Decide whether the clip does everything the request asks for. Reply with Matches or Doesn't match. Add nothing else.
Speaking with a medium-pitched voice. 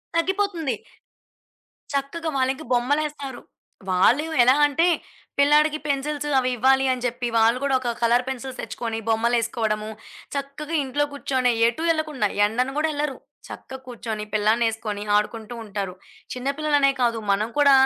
Doesn't match